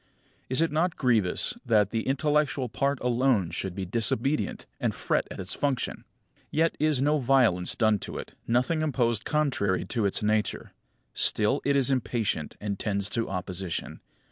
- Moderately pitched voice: No, low, 120 Hz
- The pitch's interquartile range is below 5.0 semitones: No, wide, 5.4 semitones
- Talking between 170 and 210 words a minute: No, average, 160 wpm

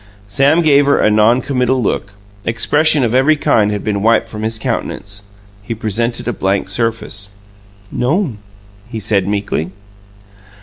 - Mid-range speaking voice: No, low, 115 Hz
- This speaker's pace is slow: No, average, 145 wpm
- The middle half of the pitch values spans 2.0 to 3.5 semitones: No, average, 3.9 semitones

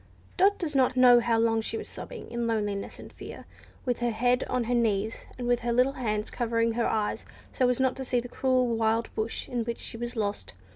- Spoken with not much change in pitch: Yes, narrow, 1.9 semitones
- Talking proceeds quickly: Yes, fast, 230 wpm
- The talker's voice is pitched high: Yes, high, 235 Hz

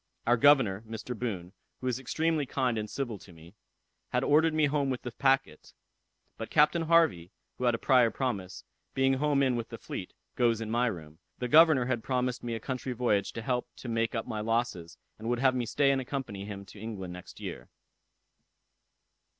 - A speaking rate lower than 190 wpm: No, average, 200 wpm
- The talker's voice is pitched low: Yes, low, 120 Hz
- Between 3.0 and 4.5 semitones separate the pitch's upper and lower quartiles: Yes, average, 3.6 semitones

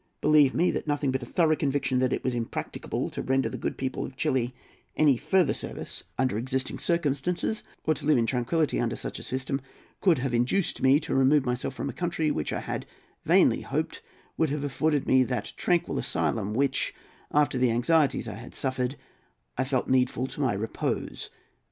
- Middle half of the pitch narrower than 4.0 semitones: Yes, average, 3.0 semitones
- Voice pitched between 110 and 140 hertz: Yes, low, 135 Hz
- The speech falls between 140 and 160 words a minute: No, average, 190 wpm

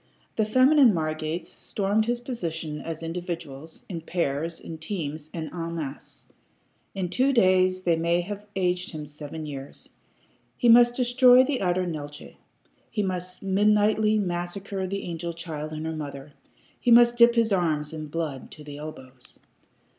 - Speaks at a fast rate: No, average, 155 wpm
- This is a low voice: No, medium, 175 Hz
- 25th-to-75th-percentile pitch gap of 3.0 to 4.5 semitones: No, average, 5.0 semitones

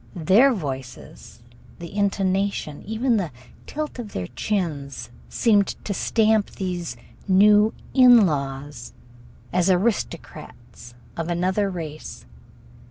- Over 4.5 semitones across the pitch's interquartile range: Yes, wide, 5.6 semitones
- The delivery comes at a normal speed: No, slow, 100 wpm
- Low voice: No, medium, 185 Hz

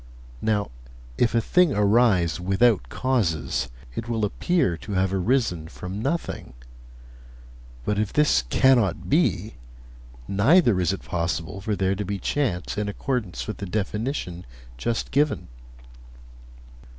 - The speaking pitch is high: No, low, 105 Hz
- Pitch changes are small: No, average, 5.2 semitones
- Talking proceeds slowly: Yes, slow, 125 wpm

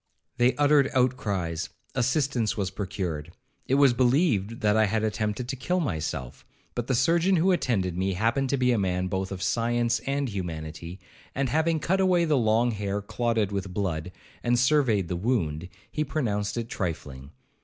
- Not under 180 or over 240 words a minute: No, average, 165 wpm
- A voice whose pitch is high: No, low, 115 Hz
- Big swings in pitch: Yes, wide, 5.8 semitones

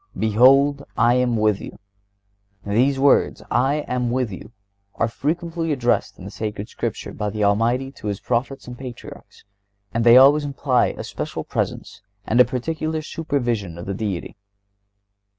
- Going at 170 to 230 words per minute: No, average, 150 wpm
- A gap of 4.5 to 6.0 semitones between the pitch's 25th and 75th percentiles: No, average, 4.1 semitones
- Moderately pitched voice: No, low, 125 Hz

